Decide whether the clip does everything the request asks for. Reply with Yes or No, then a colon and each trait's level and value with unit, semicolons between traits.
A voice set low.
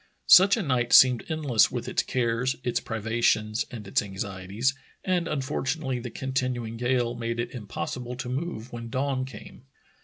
Yes: low, 125 Hz